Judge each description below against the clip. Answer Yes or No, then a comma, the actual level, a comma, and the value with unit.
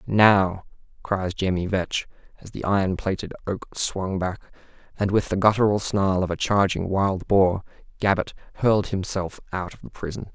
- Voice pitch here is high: No, very low, 95 Hz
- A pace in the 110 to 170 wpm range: Yes, average, 160 wpm